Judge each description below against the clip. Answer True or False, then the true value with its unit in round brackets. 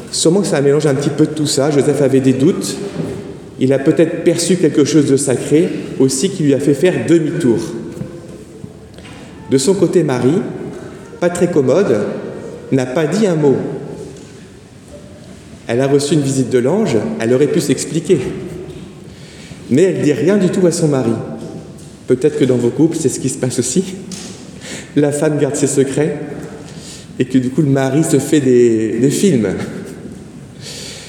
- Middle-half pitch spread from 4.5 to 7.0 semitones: False (4.1 semitones)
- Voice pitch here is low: False (150 Hz)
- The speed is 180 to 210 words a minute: False (170 wpm)